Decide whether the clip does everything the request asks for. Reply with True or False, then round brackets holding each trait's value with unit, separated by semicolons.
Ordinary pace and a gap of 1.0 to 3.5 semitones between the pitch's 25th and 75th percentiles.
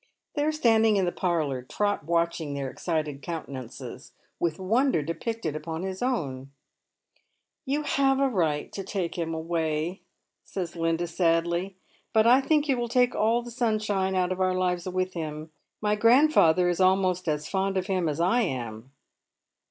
False (165 wpm; 5.2 semitones)